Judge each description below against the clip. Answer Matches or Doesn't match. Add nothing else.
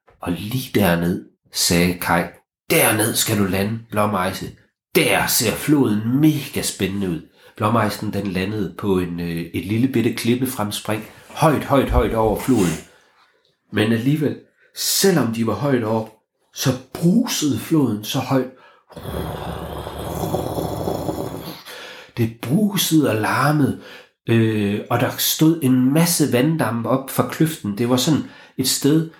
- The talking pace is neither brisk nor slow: Doesn't match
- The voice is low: Matches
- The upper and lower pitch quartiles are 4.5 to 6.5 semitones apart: Matches